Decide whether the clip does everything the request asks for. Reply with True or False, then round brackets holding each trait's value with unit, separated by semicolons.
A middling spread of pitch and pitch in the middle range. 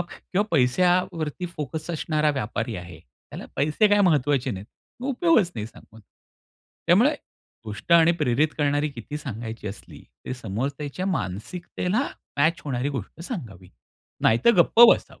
False (6.9 semitones; 145 Hz)